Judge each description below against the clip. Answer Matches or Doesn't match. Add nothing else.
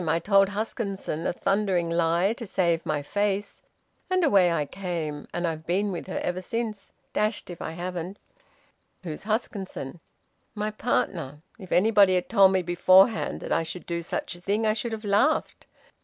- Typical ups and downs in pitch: Matches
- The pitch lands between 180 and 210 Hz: Matches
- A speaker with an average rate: Matches